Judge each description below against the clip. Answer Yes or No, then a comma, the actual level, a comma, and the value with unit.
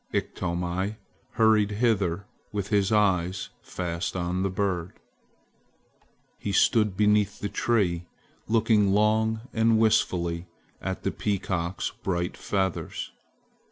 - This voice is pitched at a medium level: No, low, 100 Hz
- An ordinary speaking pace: No, slow, 105 wpm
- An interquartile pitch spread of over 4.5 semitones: No, average, 3.1 semitones